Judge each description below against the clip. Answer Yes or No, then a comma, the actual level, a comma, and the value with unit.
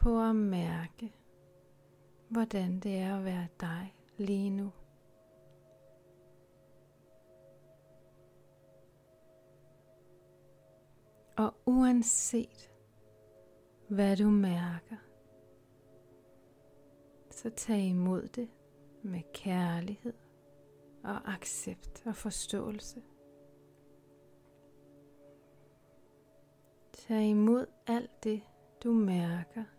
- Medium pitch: Yes, medium, 145 Hz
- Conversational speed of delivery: No, slow, 65 wpm